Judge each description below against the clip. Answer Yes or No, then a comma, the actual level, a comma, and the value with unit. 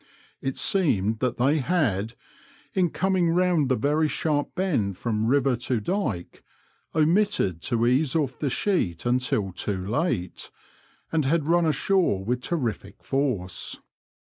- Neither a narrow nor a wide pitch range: No, wide, 7.2 semitones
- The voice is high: No, low, 135 Hz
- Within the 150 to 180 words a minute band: No, slow, 135 wpm